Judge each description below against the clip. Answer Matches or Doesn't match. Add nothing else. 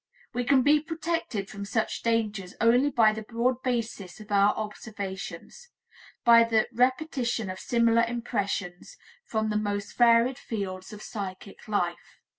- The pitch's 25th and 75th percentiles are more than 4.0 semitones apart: Doesn't match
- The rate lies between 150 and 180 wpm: Doesn't match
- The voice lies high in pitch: Matches